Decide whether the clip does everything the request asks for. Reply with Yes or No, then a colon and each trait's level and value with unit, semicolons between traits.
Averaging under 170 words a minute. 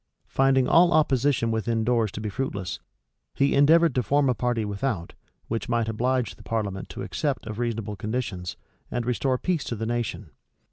No: average, 175 wpm